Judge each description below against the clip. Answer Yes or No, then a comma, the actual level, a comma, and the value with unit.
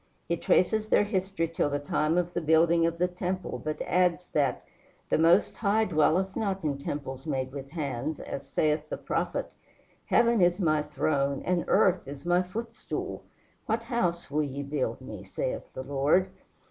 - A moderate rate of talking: Yes, average, 170 wpm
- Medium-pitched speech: Yes, medium, 165 Hz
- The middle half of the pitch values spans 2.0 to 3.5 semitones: No, average, 4.2 semitones